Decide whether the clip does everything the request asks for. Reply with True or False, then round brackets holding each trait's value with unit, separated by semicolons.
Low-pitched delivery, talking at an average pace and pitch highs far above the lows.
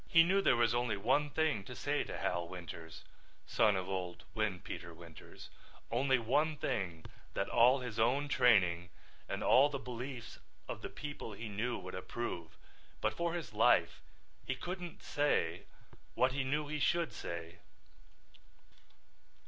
True (120 Hz; 150 wpm; 7.7 semitones)